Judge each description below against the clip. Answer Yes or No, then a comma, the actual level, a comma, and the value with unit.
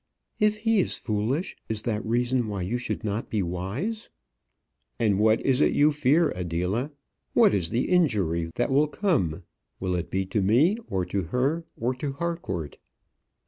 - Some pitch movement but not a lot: No, wide, 7.7 semitones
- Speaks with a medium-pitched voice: No, low, 115 Hz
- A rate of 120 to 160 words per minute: No, average, 170 wpm